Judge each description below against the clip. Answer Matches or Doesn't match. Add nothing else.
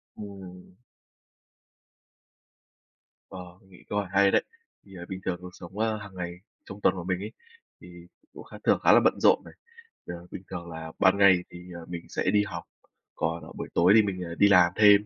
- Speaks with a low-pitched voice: Matches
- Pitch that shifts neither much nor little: Doesn't match